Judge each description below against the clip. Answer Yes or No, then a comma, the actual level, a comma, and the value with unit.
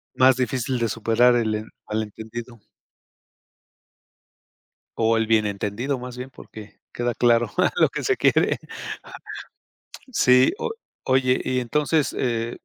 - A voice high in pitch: No, low, 120 Hz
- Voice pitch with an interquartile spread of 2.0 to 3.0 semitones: Yes, narrow, 2.4 semitones